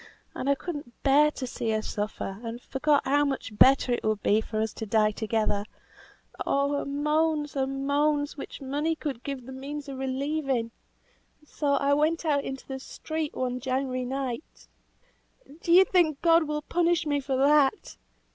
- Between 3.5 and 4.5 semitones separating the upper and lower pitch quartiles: No, average, 2.8 semitones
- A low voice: No, very high, 275 Hz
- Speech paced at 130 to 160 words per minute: No, average, 180 wpm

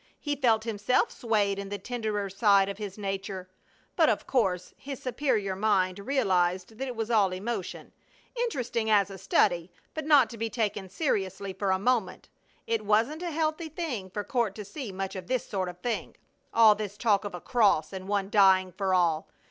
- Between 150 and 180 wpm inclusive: No, average, 190 wpm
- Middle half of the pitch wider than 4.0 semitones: No, average, 3.7 semitones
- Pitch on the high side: Yes, high, 205 Hz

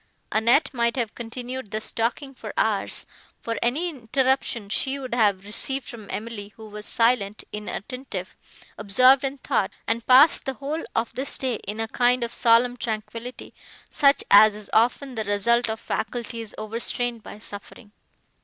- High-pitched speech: Yes, high, 235 Hz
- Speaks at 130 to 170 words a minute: Yes, average, 155 wpm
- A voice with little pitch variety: No, average, 3.0 semitones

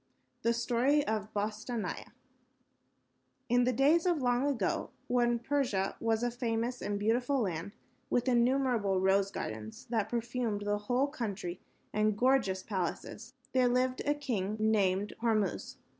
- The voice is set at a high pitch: Yes, high, 230 Hz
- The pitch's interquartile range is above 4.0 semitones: No, average, 3.4 semitones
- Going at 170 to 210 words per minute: No, average, 140 wpm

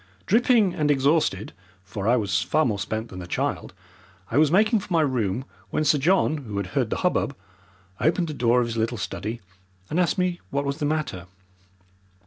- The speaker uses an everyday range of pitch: No, wide, 6.5 semitones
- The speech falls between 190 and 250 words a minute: Yes, average, 195 wpm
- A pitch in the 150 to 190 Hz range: No, medium, 140 Hz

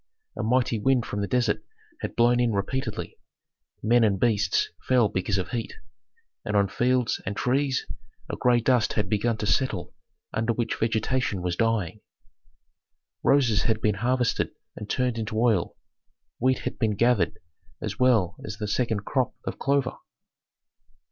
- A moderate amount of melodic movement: Yes, average, 3.0 semitones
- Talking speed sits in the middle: Yes, average, 155 wpm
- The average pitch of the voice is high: No, low, 115 Hz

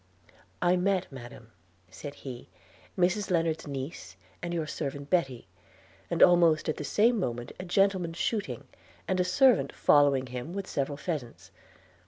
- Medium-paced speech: Yes, average, 145 wpm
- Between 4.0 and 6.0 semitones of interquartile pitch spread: Yes, average, 5.1 semitones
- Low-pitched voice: No, medium, 165 Hz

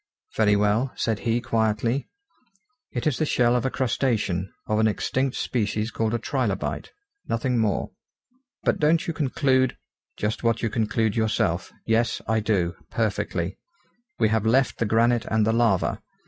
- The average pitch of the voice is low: Yes, low, 115 Hz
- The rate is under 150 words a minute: No, average, 160 wpm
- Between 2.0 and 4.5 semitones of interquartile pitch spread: Yes, narrow, 2.4 semitones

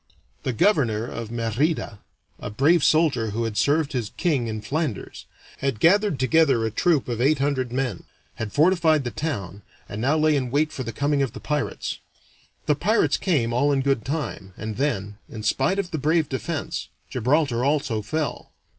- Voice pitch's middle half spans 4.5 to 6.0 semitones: Yes, average, 5.3 semitones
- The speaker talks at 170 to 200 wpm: Yes, average, 180 wpm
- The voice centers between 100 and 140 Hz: Yes, low, 135 Hz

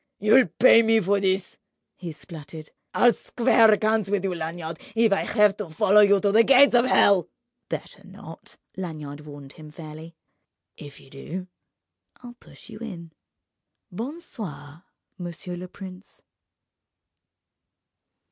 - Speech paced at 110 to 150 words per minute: Yes, average, 140 wpm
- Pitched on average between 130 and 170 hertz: No, high, 190 Hz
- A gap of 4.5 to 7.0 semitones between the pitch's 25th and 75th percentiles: Yes, average, 5.3 semitones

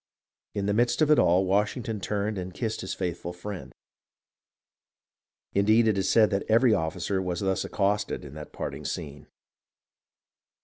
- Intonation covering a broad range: No, average, 3.3 semitones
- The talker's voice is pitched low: Yes, low, 100 Hz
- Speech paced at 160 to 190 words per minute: No, average, 150 wpm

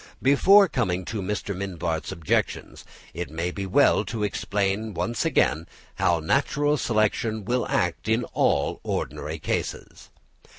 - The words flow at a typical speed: No, slow, 130 wpm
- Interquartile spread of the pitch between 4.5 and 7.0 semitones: Yes, average, 4.8 semitones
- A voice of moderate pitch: No, low, 100 Hz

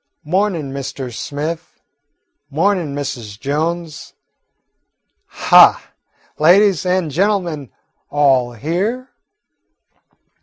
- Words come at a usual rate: No, slow, 70 wpm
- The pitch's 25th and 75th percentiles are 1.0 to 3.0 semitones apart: No, average, 4.6 semitones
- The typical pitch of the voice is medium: Yes, medium, 155 Hz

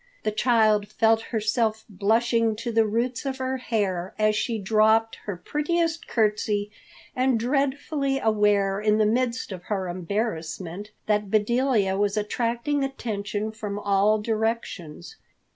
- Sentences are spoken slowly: Yes, slow, 130 wpm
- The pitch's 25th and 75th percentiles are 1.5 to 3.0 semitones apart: Yes, narrow, 2.6 semitones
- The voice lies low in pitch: No, high, 220 Hz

